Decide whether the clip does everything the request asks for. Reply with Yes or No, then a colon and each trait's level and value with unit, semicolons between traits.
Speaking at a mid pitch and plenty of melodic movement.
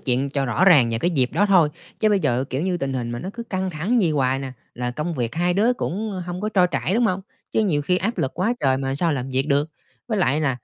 Yes: medium, 160 Hz; wide, 6.1 semitones